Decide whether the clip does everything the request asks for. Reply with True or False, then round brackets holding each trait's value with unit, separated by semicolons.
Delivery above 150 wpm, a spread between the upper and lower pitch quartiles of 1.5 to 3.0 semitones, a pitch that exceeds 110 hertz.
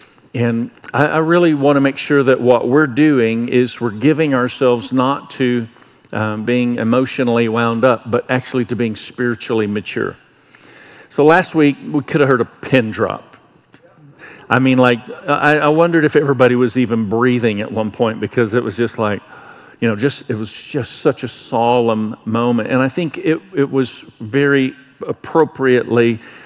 False (170 wpm; 3.4 semitones; 125 Hz)